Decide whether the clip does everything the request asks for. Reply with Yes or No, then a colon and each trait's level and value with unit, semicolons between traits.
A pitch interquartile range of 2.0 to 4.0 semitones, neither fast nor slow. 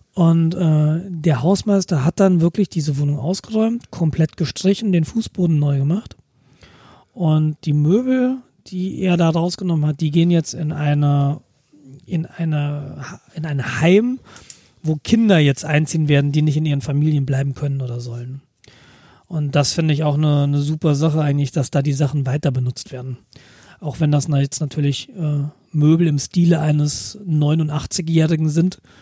Yes: average, 2.9 semitones; average, 160 wpm